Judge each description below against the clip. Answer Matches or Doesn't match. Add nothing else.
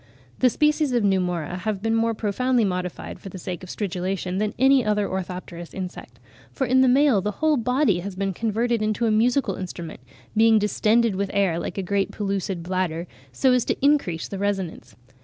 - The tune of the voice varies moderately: Matches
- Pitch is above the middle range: Matches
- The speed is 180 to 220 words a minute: Matches